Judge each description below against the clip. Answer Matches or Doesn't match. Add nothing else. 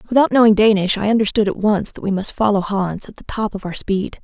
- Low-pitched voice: Doesn't match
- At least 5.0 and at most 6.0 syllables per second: Matches